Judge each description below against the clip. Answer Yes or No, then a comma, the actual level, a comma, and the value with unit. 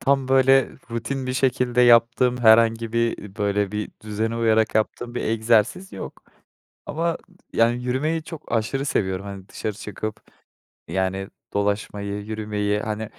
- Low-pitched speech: Yes, low, 115 Hz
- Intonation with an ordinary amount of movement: Yes, average, 3.1 semitones